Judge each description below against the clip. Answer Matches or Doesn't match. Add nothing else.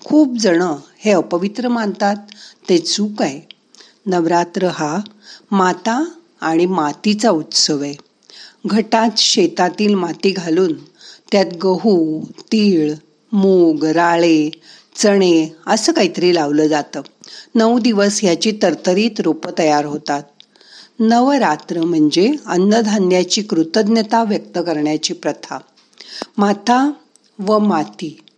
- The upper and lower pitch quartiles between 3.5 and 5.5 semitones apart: Matches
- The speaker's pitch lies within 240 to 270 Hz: Doesn't match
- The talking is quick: Doesn't match